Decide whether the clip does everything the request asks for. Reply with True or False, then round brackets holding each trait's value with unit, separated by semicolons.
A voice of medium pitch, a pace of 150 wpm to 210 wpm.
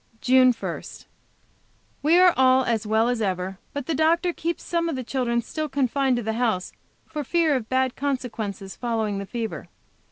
False (255 Hz; 180 wpm)